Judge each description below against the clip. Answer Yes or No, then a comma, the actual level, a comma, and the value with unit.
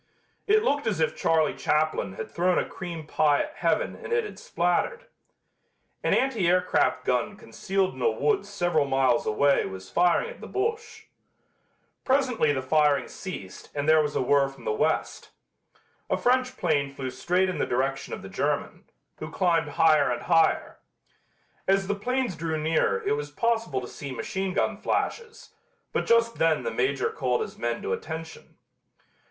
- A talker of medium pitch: Yes, medium, 160 Hz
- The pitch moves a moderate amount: No, wide, 7.7 semitones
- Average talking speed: Yes, average, 170 wpm